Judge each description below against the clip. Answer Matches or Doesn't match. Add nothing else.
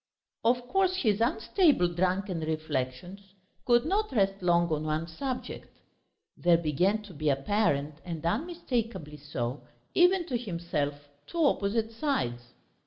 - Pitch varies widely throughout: Matches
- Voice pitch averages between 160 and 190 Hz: Matches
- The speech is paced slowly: Matches